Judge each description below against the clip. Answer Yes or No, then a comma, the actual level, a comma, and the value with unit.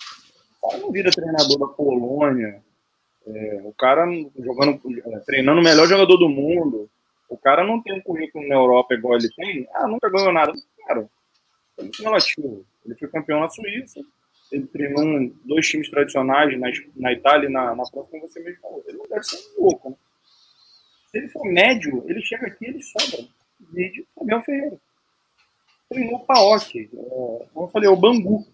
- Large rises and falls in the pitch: Yes, wide, 8.7 semitones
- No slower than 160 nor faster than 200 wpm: Yes, average, 180 wpm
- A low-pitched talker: No, medium, 165 Hz